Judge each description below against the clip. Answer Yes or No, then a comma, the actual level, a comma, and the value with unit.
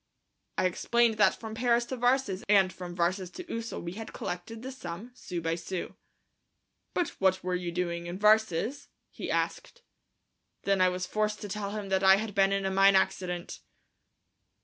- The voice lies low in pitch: No, high, 195 Hz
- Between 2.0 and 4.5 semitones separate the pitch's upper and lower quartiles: Yes, average, 3.5 semitones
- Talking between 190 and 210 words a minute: No, average, 180 wpm